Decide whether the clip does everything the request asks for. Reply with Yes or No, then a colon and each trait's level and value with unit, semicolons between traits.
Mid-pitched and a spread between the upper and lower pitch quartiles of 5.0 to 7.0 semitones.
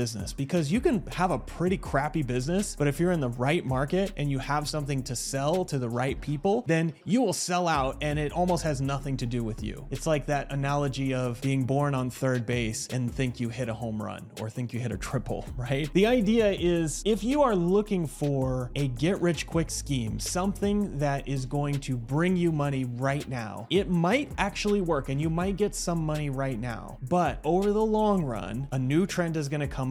Yes: medium, 145 Hz; average, 5.3 semitones